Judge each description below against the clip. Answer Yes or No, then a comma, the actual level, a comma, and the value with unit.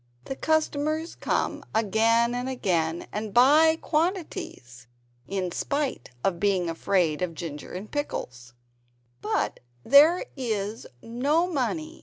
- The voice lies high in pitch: Yes, high, 210 Hz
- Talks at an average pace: No, slow, 90 wpm